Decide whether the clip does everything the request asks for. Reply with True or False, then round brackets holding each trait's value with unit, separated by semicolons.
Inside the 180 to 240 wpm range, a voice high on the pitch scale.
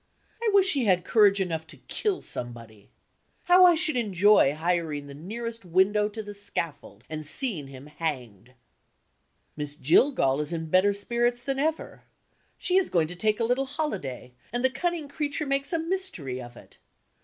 False (170 wpm; 200 Hz)